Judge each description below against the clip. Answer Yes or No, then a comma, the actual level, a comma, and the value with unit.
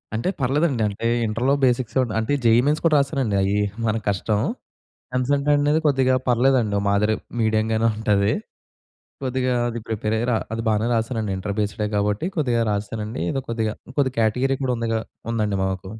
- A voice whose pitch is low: Yes, low, 115 Hz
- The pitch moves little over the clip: No, average, 3.5 semitones